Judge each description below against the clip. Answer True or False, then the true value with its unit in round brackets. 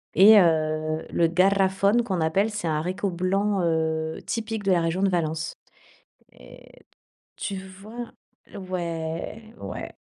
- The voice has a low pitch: False (185 Hz)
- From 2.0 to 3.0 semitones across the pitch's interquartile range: False (3.6 semitones)